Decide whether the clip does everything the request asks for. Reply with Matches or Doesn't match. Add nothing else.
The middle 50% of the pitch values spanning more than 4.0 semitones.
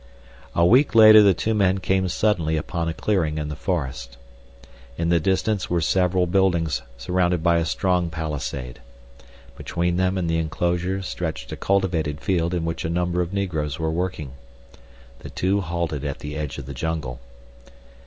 Doesn't match